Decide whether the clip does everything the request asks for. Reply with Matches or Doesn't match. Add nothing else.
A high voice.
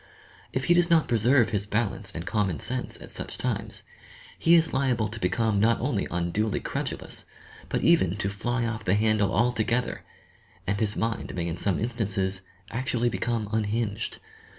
Doesn't match